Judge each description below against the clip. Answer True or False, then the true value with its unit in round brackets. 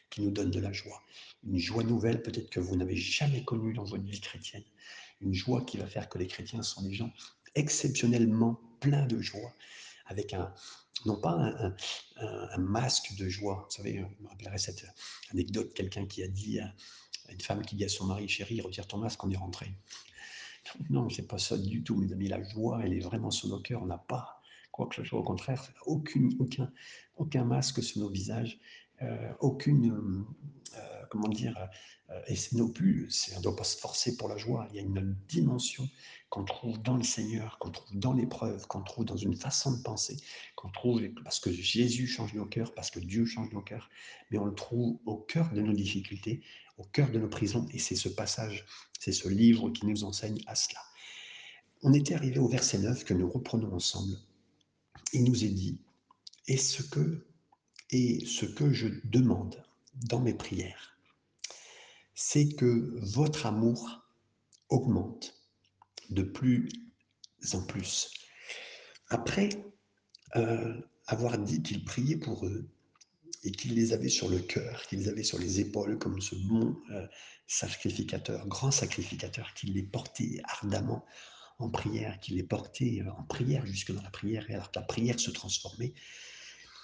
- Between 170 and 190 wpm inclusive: True (185 wpm)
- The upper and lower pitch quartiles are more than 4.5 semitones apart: False (3.8 semitones)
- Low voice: True (110 Hz)